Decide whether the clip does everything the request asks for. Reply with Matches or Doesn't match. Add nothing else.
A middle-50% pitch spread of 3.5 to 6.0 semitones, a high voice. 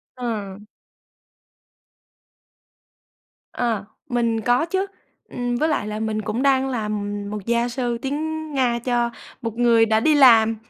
Doesn't match